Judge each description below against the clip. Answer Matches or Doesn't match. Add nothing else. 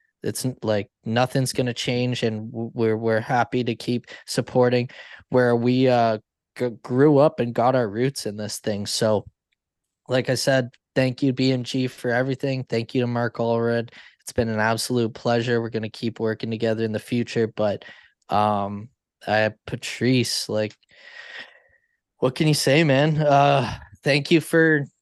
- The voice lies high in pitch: Doesn't match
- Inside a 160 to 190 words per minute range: Matches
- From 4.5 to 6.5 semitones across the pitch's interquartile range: Doesn't match